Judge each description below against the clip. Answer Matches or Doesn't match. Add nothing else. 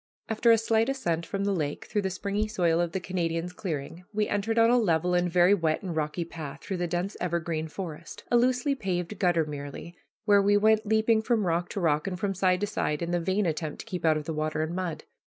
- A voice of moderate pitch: Matches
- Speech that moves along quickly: Matches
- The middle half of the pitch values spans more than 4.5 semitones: Doesn't match